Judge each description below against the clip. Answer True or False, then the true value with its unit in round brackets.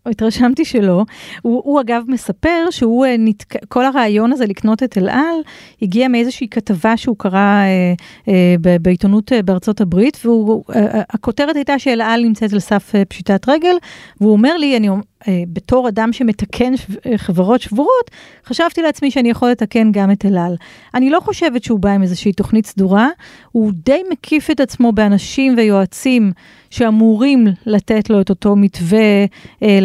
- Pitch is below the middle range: False (225 Hz)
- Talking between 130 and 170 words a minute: True (150 wpm)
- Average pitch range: True (4.1 semitones)